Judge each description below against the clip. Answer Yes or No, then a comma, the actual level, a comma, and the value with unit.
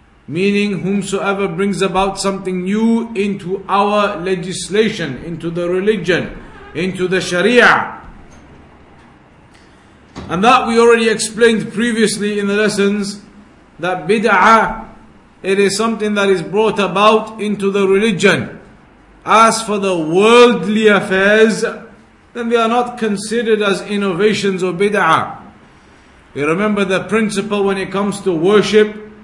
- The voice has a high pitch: Yes, high, 200 Hz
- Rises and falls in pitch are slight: Yes, narrow, 2.3 semitones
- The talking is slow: Yes, slow, 120 wpm